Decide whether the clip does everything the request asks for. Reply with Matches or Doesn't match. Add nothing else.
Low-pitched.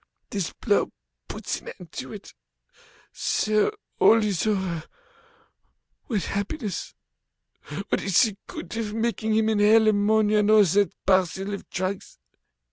Doesn't match